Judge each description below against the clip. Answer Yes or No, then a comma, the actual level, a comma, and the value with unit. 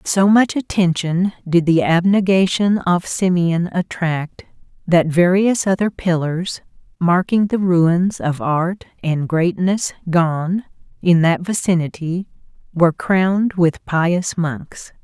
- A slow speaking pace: Yes, slow, 115 wpm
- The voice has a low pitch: No, medium, 175 Hz